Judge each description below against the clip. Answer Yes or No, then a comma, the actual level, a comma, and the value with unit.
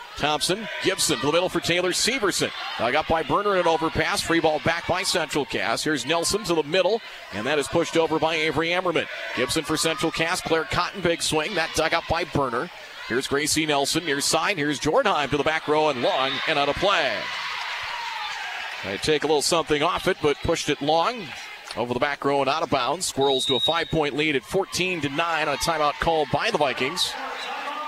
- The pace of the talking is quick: Yes, fast, 210 wpm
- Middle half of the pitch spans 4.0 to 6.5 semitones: No, average, 2.8 semitones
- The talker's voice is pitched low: No, medium, 160 Hz